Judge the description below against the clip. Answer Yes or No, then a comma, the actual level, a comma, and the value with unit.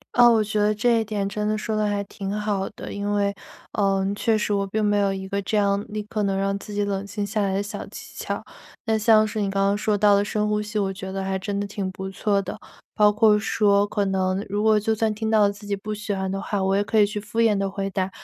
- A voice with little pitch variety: Yes, narrow, 1.3 semitones